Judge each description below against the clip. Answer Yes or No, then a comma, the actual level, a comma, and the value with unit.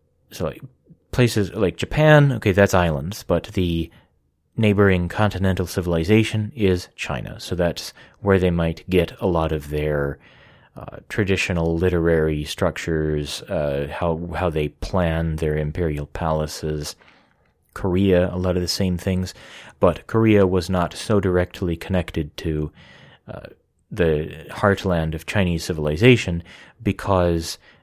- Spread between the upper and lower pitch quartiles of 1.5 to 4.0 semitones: Yes, average, 3.4 semitones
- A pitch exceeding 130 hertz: No, very low, 90 Hz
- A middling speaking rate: No, slow, 125 wpm